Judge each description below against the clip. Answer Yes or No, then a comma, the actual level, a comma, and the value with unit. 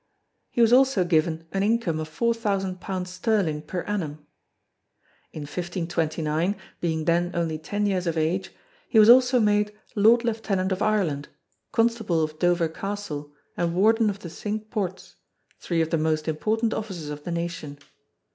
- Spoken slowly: No, average, 160 wpm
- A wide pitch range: No, average, 4.8 semitones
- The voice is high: No, medium, 180 Hz